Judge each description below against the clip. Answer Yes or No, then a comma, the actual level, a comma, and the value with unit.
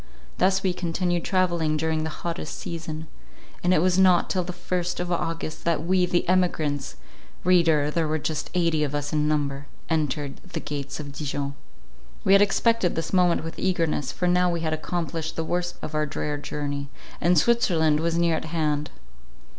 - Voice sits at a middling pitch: Yes, medium, 165 Hz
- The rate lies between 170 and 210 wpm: Yes, average, 180 wpm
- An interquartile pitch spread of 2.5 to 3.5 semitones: Yes, average, 2.8 semitones